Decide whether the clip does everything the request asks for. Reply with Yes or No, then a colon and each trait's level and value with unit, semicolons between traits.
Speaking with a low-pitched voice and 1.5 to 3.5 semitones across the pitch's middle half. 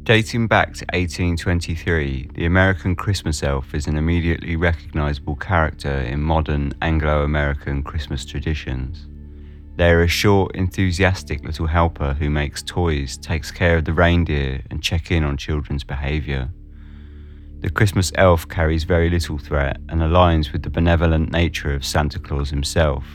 Yes: very low, 80 Hz; average, 2.7 semitones